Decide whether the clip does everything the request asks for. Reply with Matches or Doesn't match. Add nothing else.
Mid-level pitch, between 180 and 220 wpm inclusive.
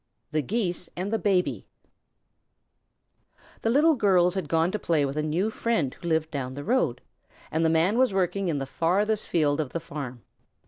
Matches